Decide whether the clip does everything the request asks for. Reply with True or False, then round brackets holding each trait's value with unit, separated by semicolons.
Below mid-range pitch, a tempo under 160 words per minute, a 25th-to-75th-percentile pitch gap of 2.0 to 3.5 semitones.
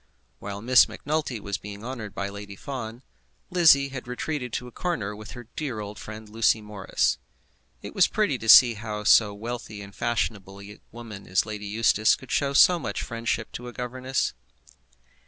False (110 Hz; 175 wpm; 3.2 semitones)